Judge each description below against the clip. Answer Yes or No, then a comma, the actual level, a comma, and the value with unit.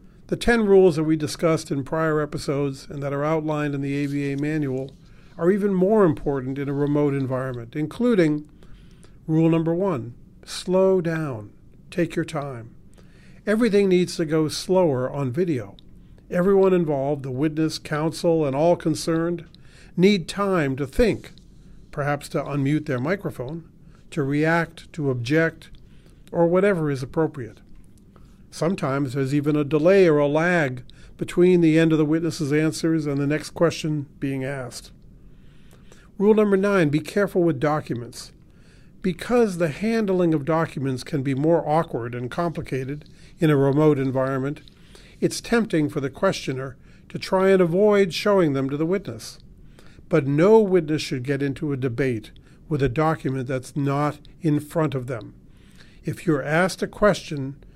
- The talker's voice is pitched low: No, medium, 155 Hz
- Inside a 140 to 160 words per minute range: Yes, average, 150 wpm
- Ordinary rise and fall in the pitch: Yes, average, 3.5 semitones